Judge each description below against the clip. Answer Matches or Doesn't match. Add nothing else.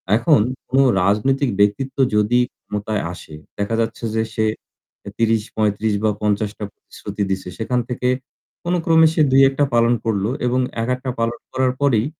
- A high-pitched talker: Doesn't match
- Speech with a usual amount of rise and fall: Matches